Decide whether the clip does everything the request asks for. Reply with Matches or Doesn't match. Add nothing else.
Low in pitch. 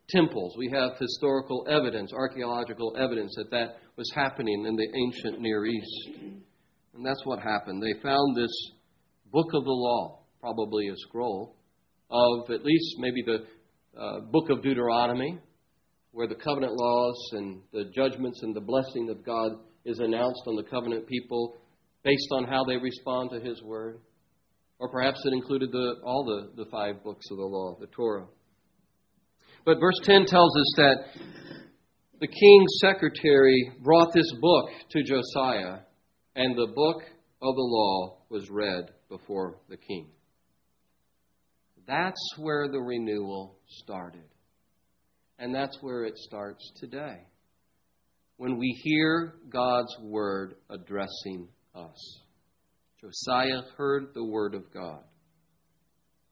Matches